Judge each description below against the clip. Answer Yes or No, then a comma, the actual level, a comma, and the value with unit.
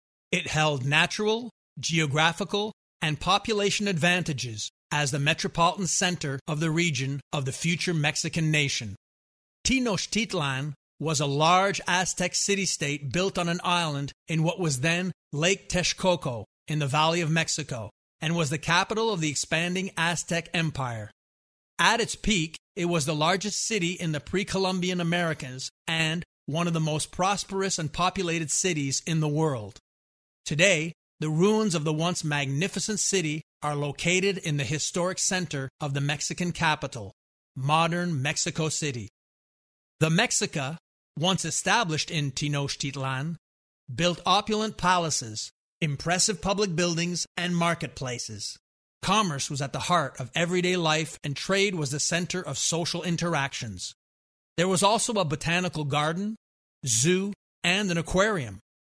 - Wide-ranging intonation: No, average, 3.9 semitones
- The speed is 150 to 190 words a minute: No, slow, 135 wpm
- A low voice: No, medium, 165 Hz